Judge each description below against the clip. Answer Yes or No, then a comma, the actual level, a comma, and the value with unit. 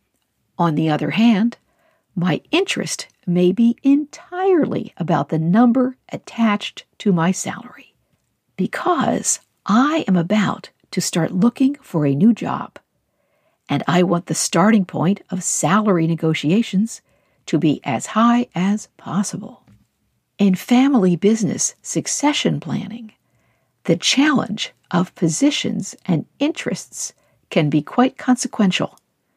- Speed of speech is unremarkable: No, slow, 115 wpm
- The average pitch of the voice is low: No, high, 205 Hz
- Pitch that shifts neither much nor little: No, wide, 5.8 semitones